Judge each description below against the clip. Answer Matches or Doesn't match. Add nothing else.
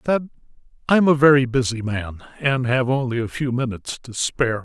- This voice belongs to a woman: Doesn't match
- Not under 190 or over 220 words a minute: Matches